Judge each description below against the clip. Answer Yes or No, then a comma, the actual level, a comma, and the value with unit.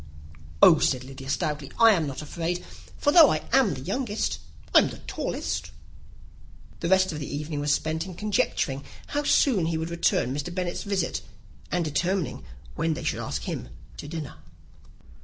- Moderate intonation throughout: Yes, average, 4.4 semitones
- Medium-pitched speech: Yes, medium, 165 Hz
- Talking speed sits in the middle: Yes, average, 170 wpm